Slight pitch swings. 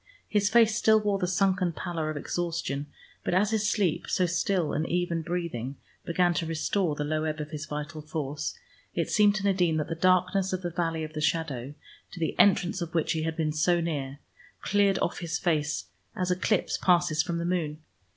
No: average, 3.0 semitones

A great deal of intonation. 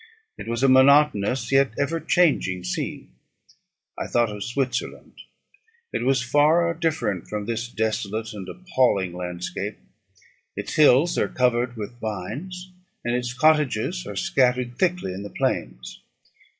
Yes: wide, 5.7 semitones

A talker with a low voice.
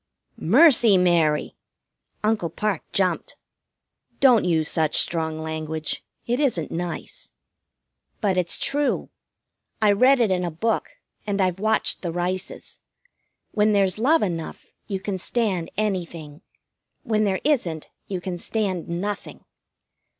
No: medium, 185 Hz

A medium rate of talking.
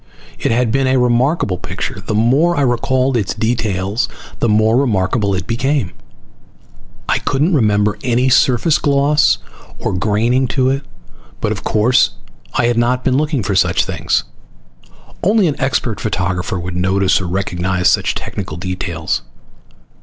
Yes: average, 145 wpm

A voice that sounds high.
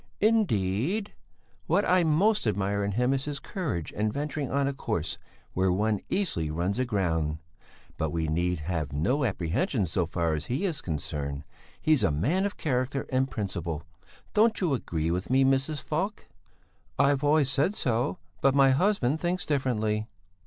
No: low, 125 Hz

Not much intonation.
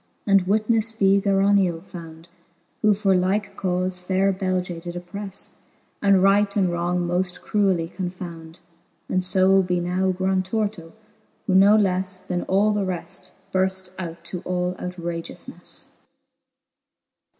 Yes: narrow, 1.7 semitones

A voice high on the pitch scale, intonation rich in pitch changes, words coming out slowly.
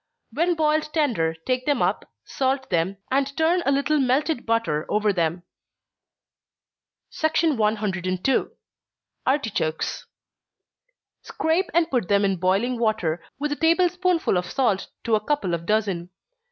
Yes: high, 240 Hz; wide, 8.0 semitones; slow, 130 wpm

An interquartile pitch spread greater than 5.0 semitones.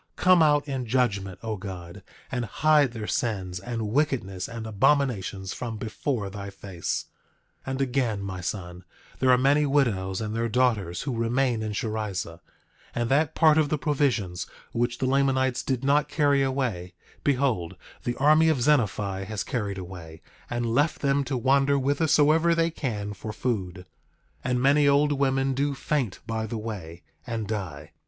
Yes: wide, 5.6 semitones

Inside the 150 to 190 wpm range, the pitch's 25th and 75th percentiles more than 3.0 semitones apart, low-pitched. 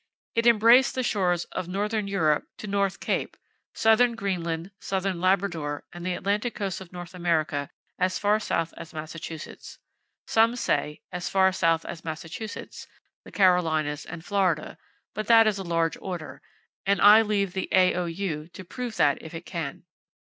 No: average, 160 wpm; average, 3.6 semitones; medium, 185 Hz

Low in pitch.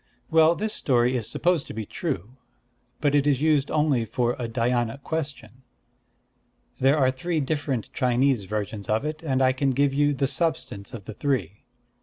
Yes: low, 130 Hz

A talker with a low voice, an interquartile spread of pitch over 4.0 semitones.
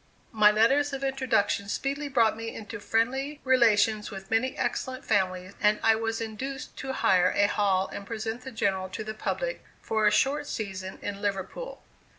No: high, 220 Hz; average, 4.4 semitones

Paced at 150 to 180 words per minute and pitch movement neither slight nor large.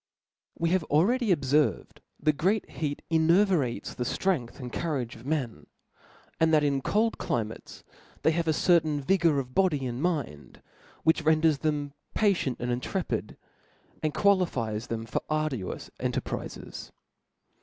No: average, 140 wpm; average, 5.0 semitones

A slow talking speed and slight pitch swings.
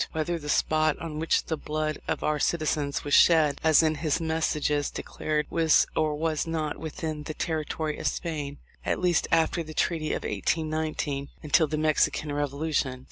No: average, 170 wpm; narrow, 1.3 semitones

